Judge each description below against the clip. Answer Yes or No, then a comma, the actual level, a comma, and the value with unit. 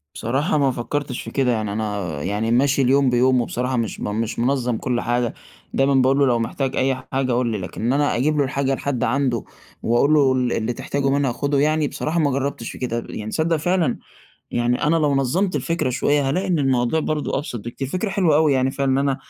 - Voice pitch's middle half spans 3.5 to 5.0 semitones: No, average, 3.0 semitones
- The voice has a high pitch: No, low, 135 Hz